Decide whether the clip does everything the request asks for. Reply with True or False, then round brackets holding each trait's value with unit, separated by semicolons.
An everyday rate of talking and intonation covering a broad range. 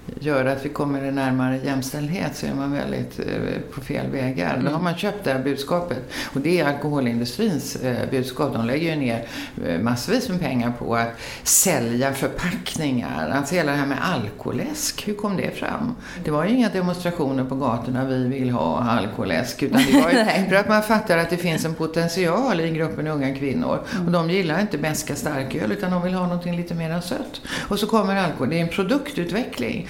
False (205 wpm; 6.3 semitones)